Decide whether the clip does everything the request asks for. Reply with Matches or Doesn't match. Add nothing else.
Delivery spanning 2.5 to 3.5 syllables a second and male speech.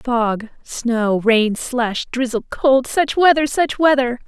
Doesn't match